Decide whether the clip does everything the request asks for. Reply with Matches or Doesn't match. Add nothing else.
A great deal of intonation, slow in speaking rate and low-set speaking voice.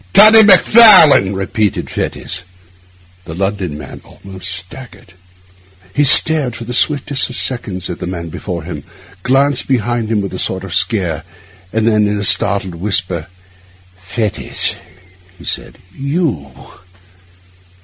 Matches